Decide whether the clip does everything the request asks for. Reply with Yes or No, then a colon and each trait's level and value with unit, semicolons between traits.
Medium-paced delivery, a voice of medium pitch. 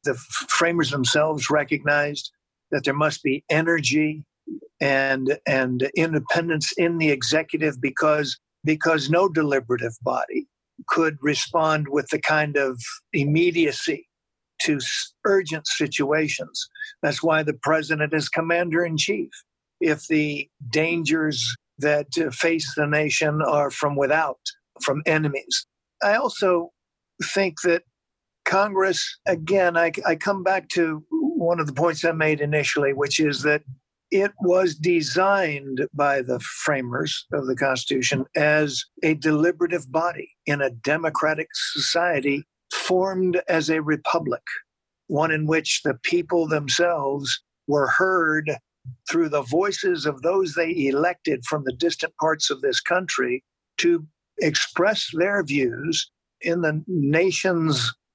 No: slow, 125 wpm; medium, 155 Hz